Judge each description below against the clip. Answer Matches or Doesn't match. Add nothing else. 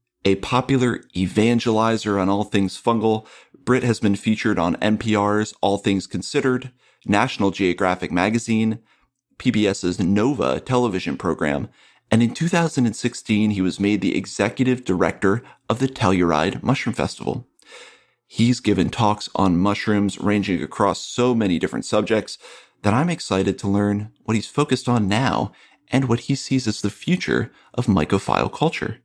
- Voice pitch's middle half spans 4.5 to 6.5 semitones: Doesn't match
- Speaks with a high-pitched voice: Doesn't match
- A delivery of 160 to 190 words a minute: Doesn't match